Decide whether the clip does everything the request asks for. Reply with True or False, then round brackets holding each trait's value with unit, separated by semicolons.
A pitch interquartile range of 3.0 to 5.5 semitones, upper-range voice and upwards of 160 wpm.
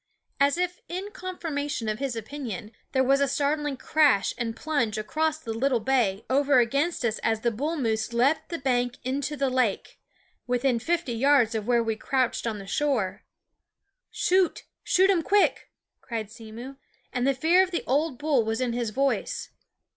True (4.6 semitones; 265 Hz; 180 wpm)